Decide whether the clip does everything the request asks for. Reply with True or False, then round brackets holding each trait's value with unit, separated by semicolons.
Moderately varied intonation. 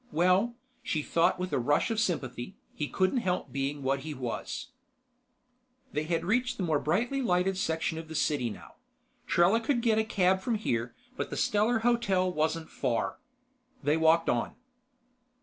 False (6.5 semitones)